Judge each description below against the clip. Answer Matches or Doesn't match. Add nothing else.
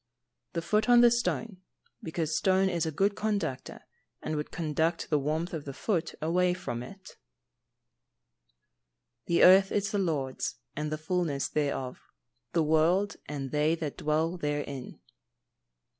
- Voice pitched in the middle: Matches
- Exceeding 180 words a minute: Doesn't match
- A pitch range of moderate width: Matches